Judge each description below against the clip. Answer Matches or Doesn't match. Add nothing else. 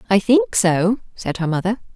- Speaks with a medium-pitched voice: Doesn't match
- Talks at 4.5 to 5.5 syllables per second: Matches